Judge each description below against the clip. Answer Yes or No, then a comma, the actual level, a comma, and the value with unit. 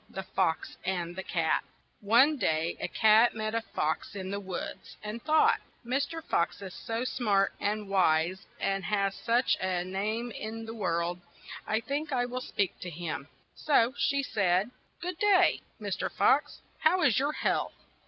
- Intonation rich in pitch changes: No, average, 4.9 semitones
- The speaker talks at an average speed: Yes, average, 180 wpm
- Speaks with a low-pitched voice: No, high, 210 Hz